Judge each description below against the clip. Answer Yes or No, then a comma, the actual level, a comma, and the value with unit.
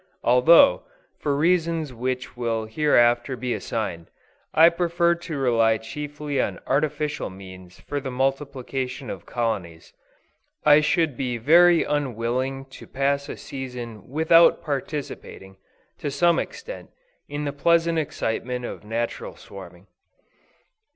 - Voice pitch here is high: No, low, 135 Hz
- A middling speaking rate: No, slow, 120 wpm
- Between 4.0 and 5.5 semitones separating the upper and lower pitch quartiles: Yes, average, 4.3 semitones